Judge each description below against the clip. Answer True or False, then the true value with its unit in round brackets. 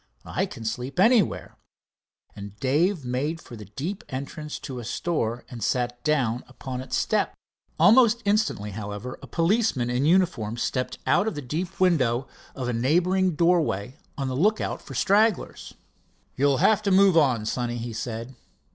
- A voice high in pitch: False (135 Hz)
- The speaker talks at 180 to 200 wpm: False (160 wpm)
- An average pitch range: False (7.0 semitones)